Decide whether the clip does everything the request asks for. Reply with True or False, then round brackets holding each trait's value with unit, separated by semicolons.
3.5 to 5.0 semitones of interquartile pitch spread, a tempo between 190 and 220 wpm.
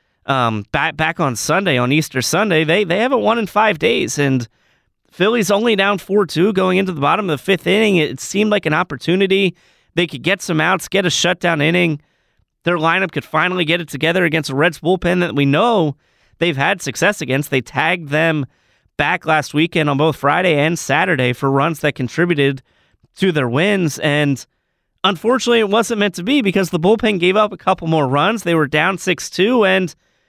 True (4.7 semitones; 205 wpm)